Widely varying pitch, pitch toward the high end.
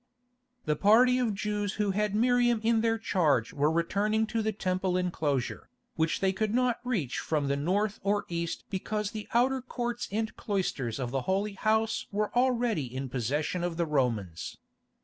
Yes: wide, 6.1 semitones; high, 200 Hz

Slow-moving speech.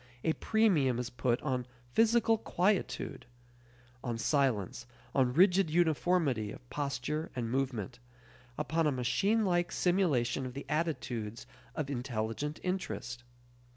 Yes: slow, 120 wpm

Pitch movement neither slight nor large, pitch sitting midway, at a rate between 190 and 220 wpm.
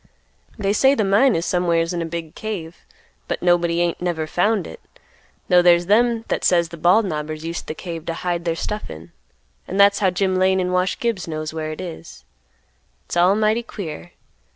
Yes: average, 3.2 semitones; medium, 175 Hz; average, 200 wpm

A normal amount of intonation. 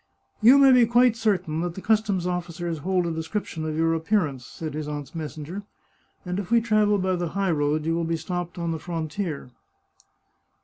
Yes: average, 4.2 semitones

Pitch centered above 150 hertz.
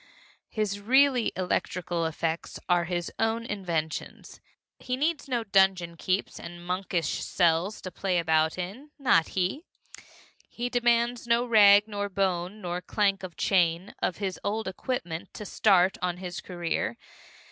Yes: high, 190 Hz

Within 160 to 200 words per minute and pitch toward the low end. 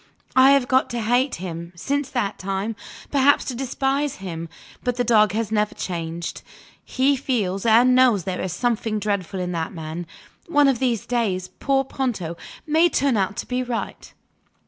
No: average, 170 wpm; high, 230 Hz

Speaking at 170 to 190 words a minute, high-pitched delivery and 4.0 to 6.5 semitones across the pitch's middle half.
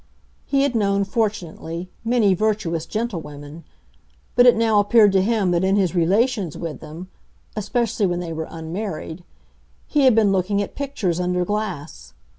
No: average, 155 wpm; high, 195 Hz; average, 4.5 semitones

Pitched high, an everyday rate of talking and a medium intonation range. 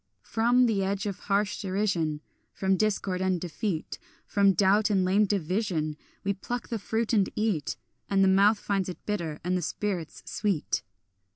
No: high, 195 Hz; average, 165 wpm; narrow, 2.3 semitones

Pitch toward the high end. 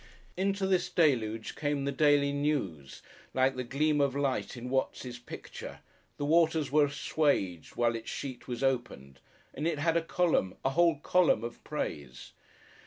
No: medium, 140 Hz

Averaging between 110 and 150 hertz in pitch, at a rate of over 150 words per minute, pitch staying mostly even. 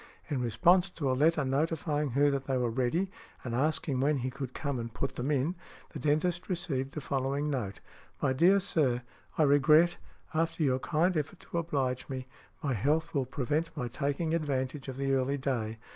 No: medium, 140 Hz; average, 190 wpm; average, 3.4 semitones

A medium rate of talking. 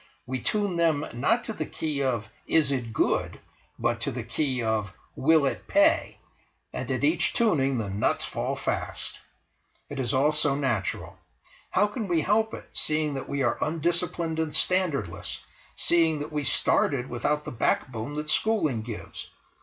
Yes: average, 165 wpm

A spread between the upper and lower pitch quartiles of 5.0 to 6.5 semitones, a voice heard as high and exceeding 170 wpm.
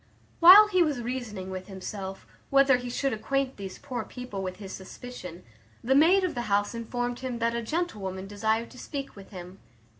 Yes: wide, 5.6 semitones; high, 235 Hz; average, 185 wpm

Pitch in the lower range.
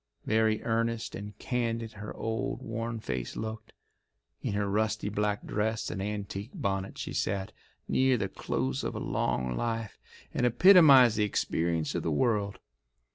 Yes: low, 110 Hz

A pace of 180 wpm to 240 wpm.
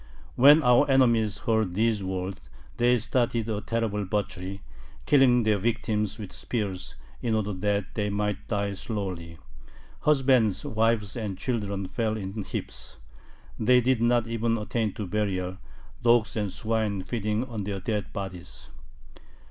No: average, 140 wpm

